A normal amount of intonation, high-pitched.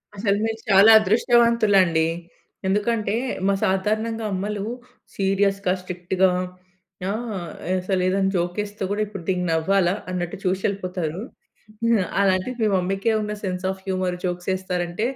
No: narrow, 2.3 semitones; high, 195 Hz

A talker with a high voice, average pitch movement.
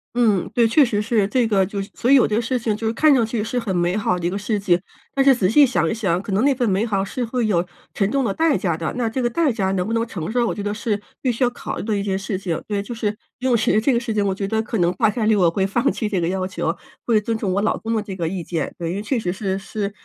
Yes: high, 210 Hz; average, 3.5 semitones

